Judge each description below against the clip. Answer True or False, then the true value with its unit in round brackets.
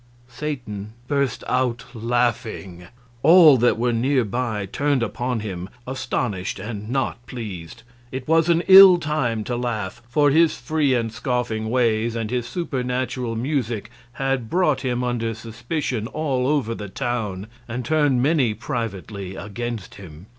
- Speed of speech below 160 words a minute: True (140 wpm)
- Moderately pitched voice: False (120 Hz)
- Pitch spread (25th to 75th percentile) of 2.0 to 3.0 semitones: False (3.5 semitones)